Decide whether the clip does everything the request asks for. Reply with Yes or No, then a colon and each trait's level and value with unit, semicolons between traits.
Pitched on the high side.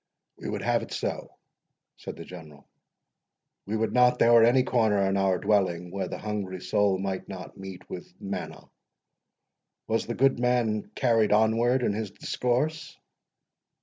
No: low, 105 Hz